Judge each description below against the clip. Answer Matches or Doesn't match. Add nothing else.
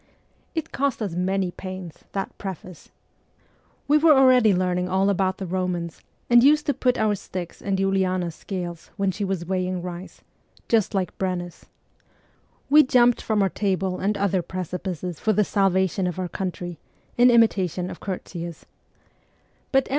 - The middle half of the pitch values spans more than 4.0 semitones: Doesn't match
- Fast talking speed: Doesn't match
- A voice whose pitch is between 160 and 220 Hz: Matches